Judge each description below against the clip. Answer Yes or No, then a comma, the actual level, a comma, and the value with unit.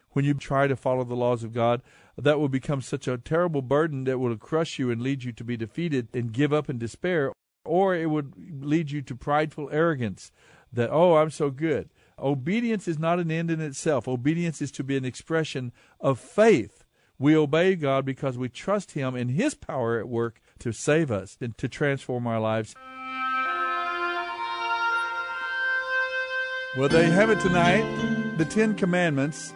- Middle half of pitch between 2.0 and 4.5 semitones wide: No, average, 5.1 semitones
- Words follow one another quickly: No, average, 175 wpm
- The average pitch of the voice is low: No, medium, 145 Hz